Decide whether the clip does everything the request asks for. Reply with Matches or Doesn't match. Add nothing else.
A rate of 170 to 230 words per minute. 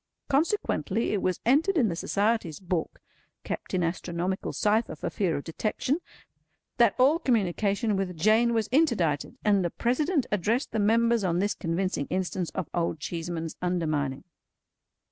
Doesn't match